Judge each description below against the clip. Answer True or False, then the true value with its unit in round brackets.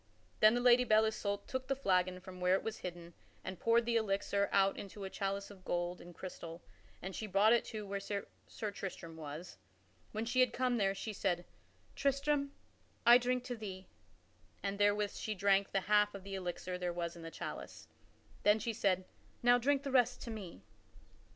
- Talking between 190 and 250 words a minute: True (195 wpm)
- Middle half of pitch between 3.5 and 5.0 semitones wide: True (3.8 semitones)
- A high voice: True (200 Hz)